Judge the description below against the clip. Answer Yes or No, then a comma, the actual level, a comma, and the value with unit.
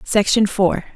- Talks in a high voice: Yes, high, 195 Hz